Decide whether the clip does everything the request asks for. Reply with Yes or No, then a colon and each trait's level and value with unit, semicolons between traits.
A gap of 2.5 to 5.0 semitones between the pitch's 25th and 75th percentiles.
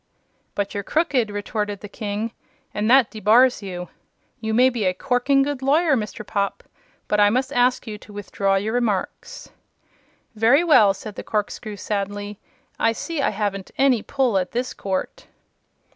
Yes: average, 3.8 semitones